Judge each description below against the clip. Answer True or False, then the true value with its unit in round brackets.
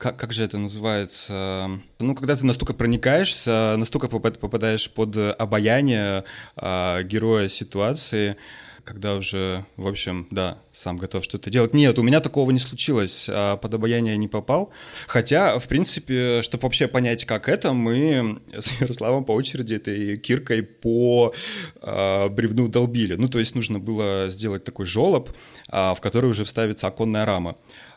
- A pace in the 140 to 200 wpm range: True (145 wpm)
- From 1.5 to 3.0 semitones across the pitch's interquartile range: False (3.5 semitones)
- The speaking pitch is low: True (110 Hz)